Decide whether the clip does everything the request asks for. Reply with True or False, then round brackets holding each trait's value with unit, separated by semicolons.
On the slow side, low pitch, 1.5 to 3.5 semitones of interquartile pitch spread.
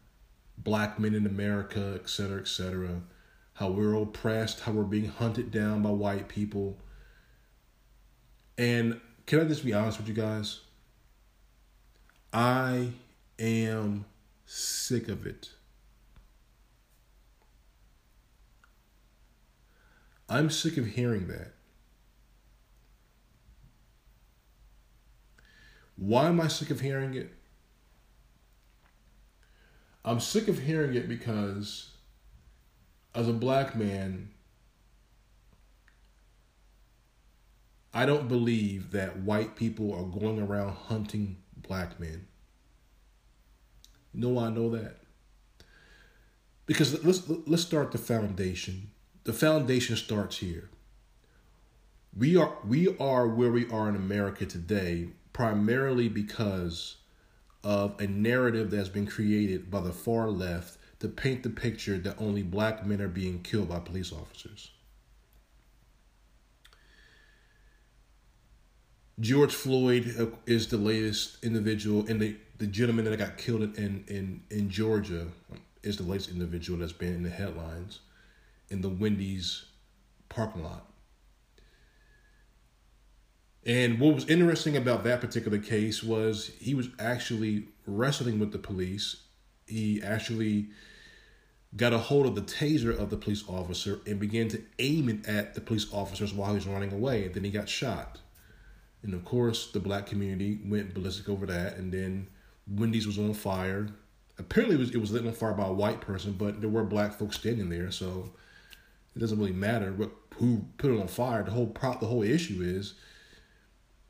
True (130 wpm; 105 Hz; 2.9 semitones)